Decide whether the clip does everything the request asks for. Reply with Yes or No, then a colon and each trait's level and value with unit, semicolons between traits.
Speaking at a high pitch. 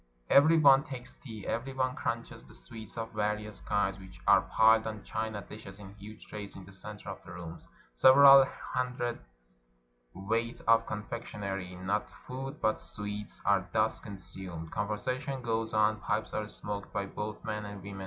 No: low, 105 Hz